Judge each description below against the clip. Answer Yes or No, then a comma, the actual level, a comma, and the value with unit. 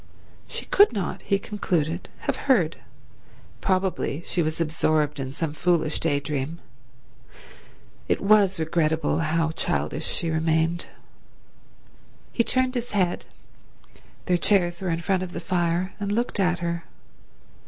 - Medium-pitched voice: Yes, medium, 170 Hz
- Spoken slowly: Yes, slow, 125 wpm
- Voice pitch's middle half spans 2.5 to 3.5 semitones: Yes, average, 3.1 semitones